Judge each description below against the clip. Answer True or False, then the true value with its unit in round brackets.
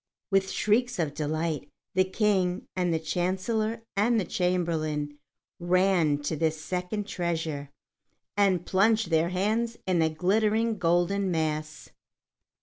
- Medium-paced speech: False (125 wpm)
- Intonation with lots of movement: False (4.0 semitones)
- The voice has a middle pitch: True (180 Hz)